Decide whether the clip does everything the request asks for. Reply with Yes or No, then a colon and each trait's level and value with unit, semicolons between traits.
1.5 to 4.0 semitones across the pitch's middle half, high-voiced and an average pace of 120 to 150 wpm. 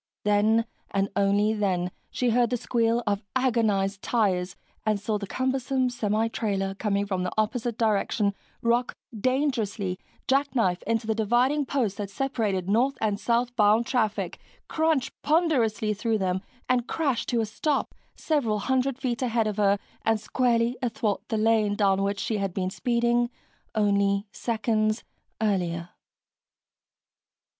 Yes: average, 3.3 semitones; high, 220 Hz; average, 140 wpm